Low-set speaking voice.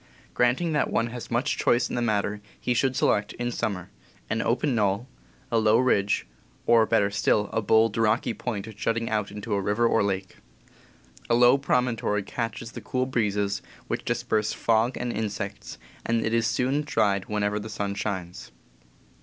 Yes: low, 110 Hz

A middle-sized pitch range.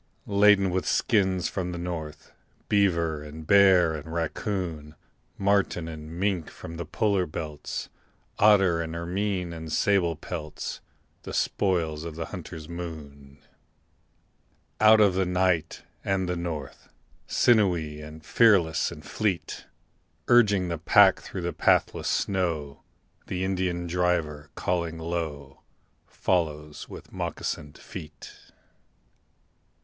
Yes: average, 3.3 semitones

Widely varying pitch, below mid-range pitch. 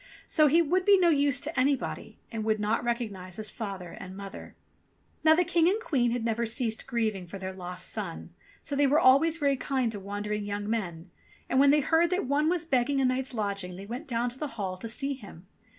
No: wide, 5.9 semitones; high, 240 Hz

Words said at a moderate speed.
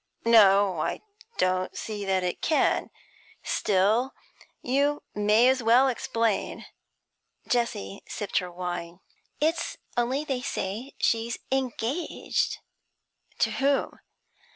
No: slow, 105 wpm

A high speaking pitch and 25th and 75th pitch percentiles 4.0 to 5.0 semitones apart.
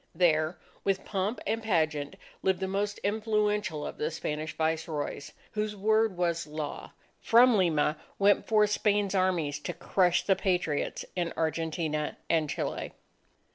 No: medium, 180 Hz; average, 4.7 semitones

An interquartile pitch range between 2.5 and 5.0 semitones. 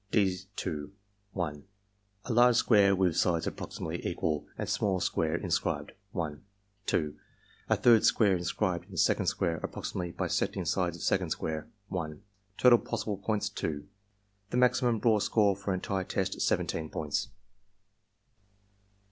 Yes: average, 4.2 semitones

